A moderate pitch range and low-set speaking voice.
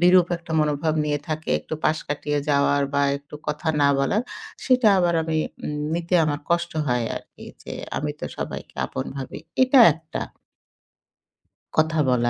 No: average, 3.1 semitones; medium, 155 Hz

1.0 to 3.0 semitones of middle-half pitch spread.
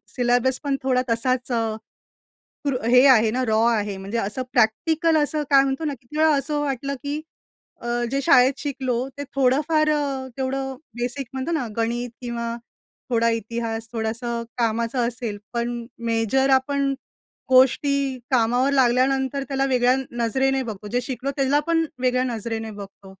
Yes: average, 2.7 semitones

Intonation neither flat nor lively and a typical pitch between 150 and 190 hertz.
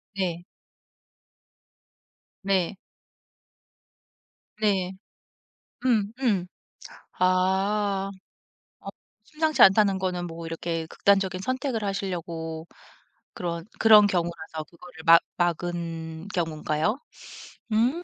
Yes: average, 3.3 semitones; medium, 185 Hz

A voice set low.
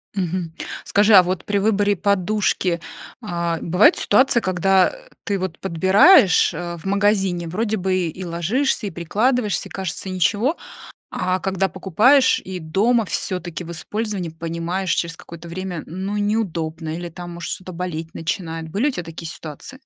No: medium, 185 Hz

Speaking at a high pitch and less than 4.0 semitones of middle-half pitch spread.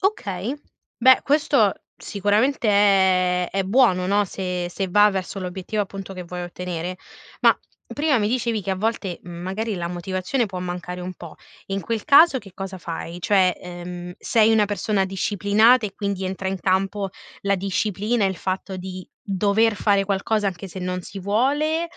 Yes: high, 195 Hz; average, 2.7 semitones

